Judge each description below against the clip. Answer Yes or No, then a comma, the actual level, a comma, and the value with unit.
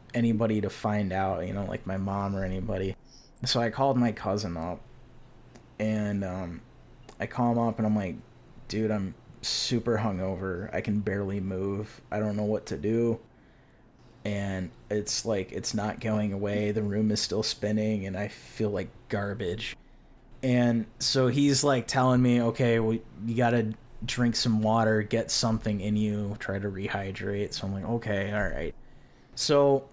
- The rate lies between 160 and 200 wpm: Yes, average, 170 wpm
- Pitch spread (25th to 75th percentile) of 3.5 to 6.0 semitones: No, average, 2.8 semitones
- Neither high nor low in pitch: No, low, 110 Hz